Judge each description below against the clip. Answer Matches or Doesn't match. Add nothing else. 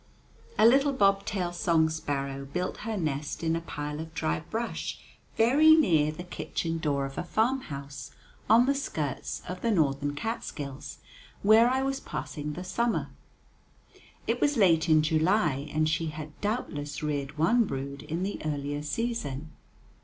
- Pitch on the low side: Doesn't match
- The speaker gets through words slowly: Doesn't match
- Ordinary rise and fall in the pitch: Doesn't match